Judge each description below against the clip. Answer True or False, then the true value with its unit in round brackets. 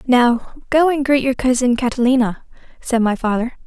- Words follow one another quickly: False (165 wpm)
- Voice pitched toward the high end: True (250 Hz)